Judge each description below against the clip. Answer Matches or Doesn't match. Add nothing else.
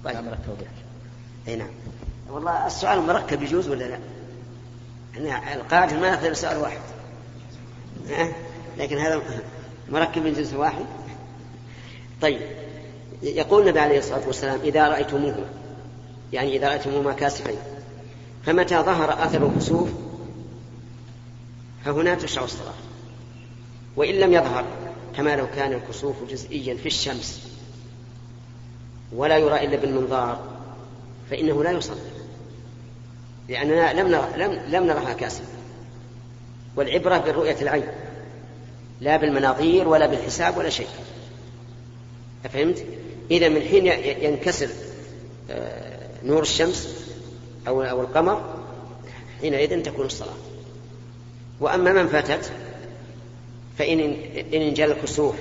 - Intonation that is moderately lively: Matches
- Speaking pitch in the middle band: Doesn't match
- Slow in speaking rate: Doesn't match